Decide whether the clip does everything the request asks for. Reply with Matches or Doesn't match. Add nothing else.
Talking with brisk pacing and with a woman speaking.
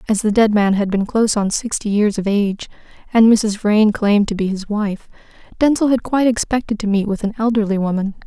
Matches